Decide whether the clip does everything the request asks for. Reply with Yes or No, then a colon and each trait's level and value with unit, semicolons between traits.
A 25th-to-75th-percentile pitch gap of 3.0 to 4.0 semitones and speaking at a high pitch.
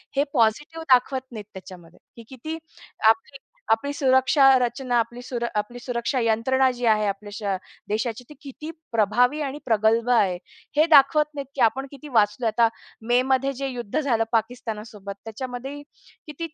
Yes: average, 3.7 semitones; high, 245 Hz